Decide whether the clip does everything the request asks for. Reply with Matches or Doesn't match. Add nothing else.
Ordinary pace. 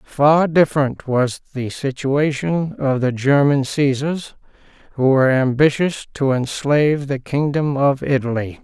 Doesn't match